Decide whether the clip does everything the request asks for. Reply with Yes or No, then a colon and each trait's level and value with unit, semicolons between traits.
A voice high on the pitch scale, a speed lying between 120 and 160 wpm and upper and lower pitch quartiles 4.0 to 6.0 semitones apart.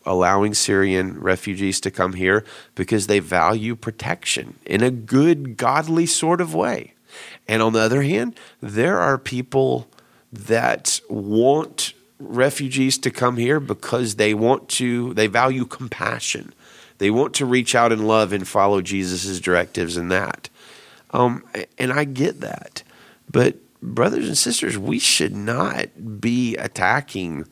No: low, 110 Hz; average, 140 wpm; average, 4.8 semitones